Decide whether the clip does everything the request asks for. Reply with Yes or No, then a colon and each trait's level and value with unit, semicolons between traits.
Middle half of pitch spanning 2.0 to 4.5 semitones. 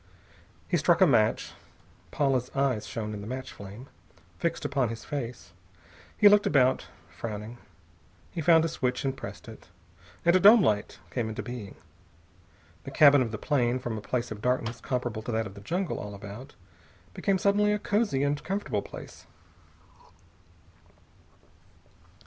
No: average, 5.1 semitones